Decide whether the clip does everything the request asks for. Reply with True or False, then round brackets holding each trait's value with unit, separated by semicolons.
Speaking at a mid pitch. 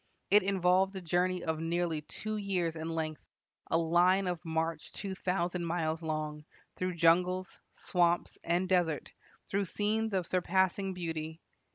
True (175 Hz)